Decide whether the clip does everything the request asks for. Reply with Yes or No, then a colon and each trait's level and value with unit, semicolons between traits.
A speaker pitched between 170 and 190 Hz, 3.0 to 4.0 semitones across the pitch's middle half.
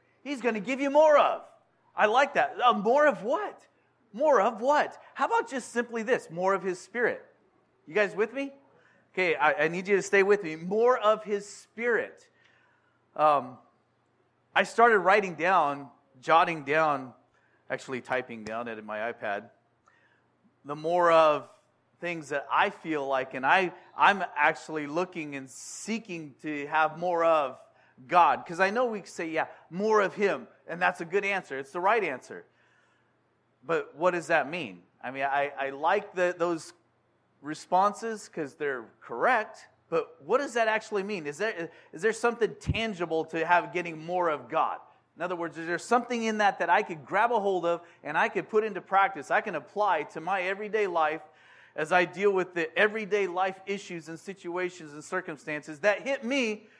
No: medium, 185 Hz; average, 5.3 semitones